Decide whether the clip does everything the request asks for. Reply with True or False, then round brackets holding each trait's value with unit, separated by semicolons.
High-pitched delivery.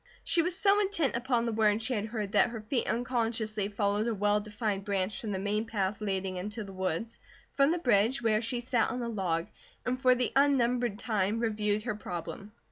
True (220 Hz)